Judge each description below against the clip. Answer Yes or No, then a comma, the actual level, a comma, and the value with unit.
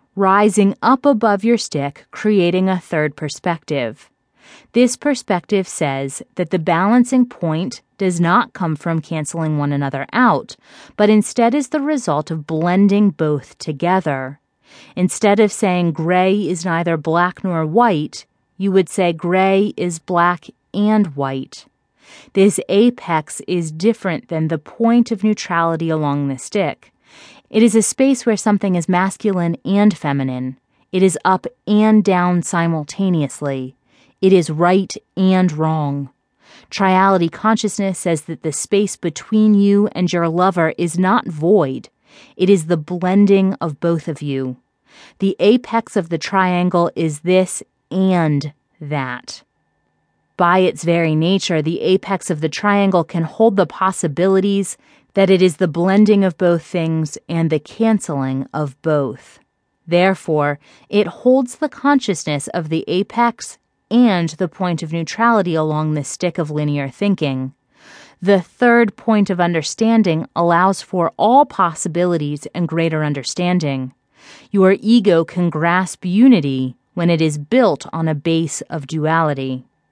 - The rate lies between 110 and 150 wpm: Yes, average, 140 wpm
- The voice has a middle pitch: Yes, medium, 180 Hz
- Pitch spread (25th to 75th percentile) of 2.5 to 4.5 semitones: Yes, average, 4.0 semitones